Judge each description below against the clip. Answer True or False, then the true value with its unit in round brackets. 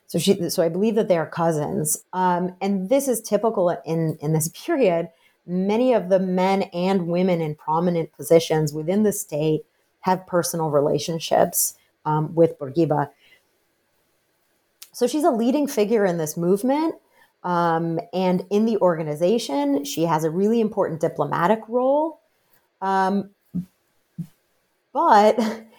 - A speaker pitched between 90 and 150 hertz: False (180 Hz)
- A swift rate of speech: False (135 wpm)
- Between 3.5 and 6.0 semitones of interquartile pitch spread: True (4.3 semitones)